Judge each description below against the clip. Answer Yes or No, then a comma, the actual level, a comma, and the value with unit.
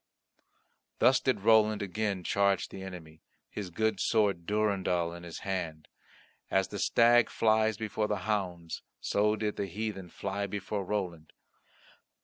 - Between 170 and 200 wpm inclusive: No, slow, 135 wpm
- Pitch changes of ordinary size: Yes, average, 3.1 semitones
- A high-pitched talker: No, low, 100 Hz